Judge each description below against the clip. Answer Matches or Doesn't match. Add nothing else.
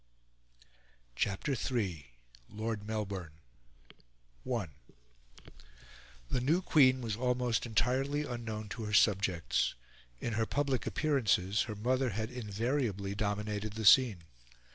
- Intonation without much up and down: Doesn't match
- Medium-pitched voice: Doesn't match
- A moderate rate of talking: Doesn't match